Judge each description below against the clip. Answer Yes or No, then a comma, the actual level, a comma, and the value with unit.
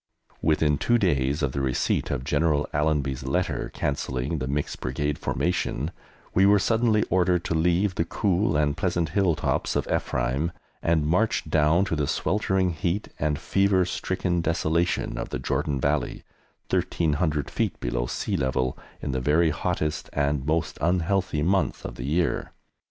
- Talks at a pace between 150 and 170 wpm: Yes, average, 155 wpm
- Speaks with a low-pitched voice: Yes, very low, 80 Hz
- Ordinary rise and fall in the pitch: Yes, average, 3.9 semitones